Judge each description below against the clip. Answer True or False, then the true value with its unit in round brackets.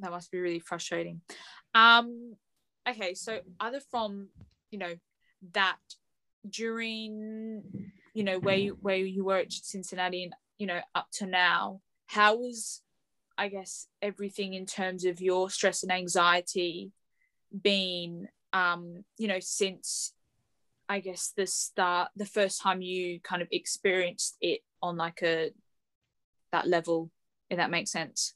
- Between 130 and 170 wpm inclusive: True (140 wpm)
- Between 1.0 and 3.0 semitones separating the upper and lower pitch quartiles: True (2.5 semitones)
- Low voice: False (190 Hz)